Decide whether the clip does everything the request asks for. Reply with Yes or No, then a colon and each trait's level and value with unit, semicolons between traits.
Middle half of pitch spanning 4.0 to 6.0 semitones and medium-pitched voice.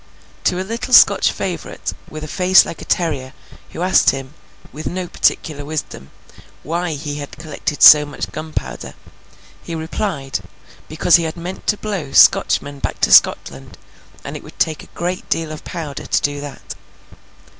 No: average, 3.4 semitones; medium, 155 Hz